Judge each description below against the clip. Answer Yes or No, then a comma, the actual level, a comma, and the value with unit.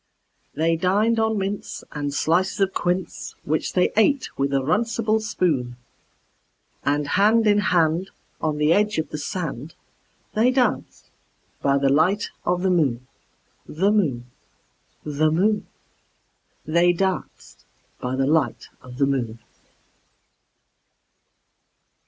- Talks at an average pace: No, slow, 120 wpm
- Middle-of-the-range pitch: Yes, medium, 170 Hz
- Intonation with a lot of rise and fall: Yes, wide, 6.1 semitones